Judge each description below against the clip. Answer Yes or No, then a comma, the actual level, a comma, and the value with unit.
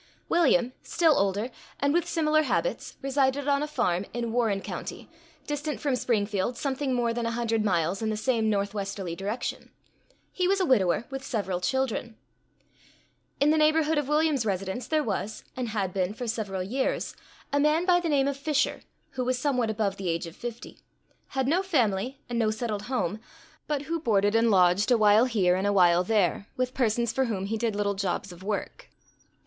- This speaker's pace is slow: No, average, 190 wpm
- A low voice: No, high, 235 Hz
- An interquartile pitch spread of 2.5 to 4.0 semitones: No, wide, 5.4 semitones